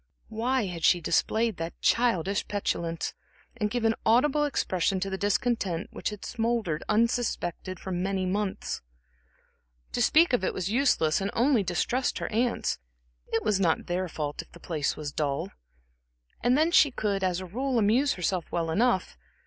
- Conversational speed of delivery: Yes, average, 165 wpm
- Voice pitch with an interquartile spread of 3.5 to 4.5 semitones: No, average, 5.2 semitones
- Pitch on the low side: No, high, 200 Hz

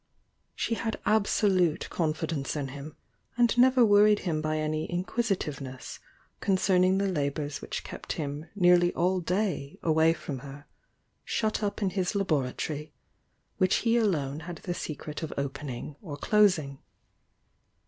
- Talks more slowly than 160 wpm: Yes, average, 145 wpm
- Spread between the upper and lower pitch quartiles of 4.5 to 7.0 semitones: Yes, average, 5.2 semitones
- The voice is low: No, medium, 170 Hz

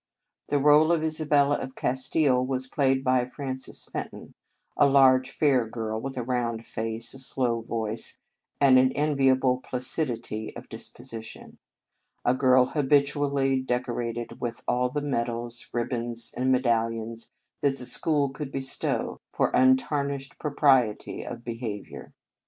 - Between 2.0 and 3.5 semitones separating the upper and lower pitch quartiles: Yes, average, 2.8 semitones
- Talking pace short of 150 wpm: Yes, average, 140 wpm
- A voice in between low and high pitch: No, low, 130 Hz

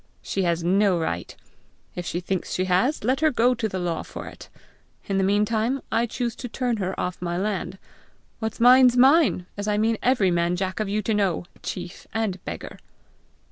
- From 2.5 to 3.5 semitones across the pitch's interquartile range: No, average, 4.5 semitones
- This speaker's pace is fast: No, average, 195 wpm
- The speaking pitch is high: Yes, high, 205 Hz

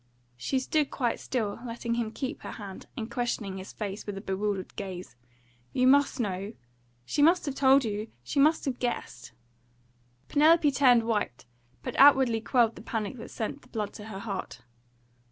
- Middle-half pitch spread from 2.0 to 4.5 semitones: No, average, 4.9 semitones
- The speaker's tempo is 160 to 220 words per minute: Yes, average, 175 wpm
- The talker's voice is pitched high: Yes, high, 225 Hz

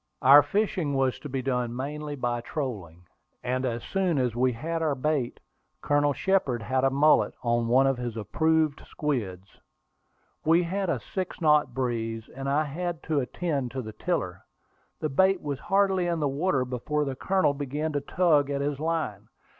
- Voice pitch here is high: No, medium, 140 Hz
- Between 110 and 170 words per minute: No, average, 180 wpm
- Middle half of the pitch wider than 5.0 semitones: No, average, 4.1 semitones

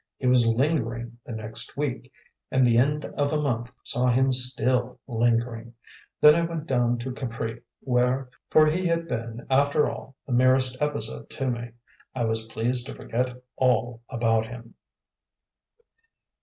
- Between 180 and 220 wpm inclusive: No, average, 155 wpm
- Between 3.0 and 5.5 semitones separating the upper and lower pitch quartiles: No, narrow, 2.4 semitones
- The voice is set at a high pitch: No, low, 125 Hz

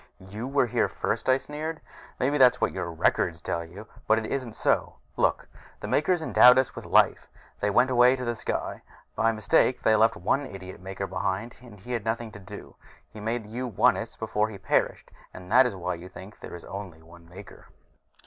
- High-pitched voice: No, low, 110 Hz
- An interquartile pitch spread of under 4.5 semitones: No, average, 4.8 semitones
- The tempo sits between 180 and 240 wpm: Yes, fast, 205 wpm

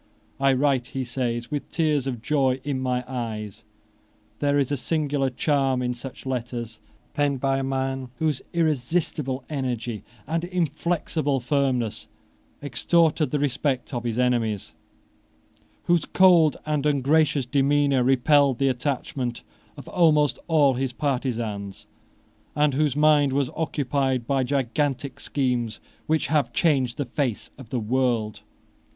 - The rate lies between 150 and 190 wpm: No, slow, 135 wpm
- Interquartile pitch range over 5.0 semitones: No, average, 2.9 semitones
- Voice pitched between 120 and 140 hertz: Yes, low, 135 Hz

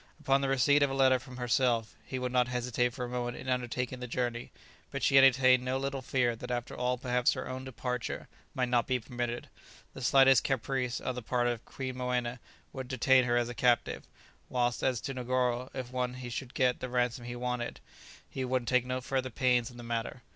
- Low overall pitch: Yes, low, 125 Hz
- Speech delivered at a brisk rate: Yes, fast, 215 wpm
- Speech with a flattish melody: Yes, narrow, 1.1 semitones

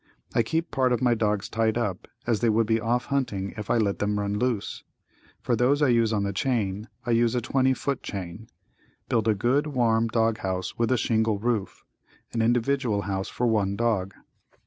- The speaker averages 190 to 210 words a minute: Yes, average, 200 wpm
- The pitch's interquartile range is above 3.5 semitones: No, average, 3.0 semitones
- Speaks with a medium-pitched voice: No, low, 115 Hz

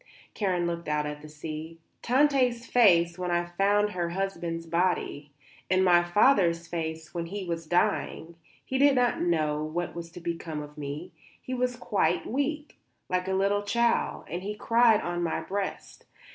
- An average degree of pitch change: Yes, average, 3.8 semitones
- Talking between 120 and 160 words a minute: No, average, 170 wpm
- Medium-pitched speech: Yes, medium, 175 Hz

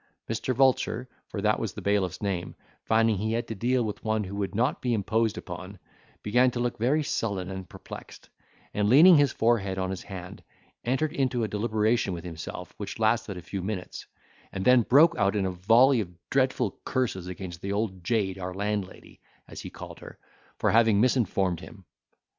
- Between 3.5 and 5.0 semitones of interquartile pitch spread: Yes, average, 4.0 semitones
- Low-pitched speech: Yes, low, 105 Hz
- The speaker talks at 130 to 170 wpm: No, average, 190 wpm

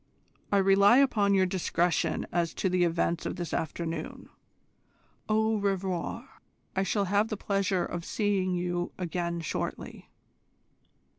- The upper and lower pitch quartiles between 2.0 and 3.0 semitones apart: Yes, narrow, 2.5 semitones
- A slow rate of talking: Yes, slow, 130 wpm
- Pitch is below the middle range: No, medium, 185 Hz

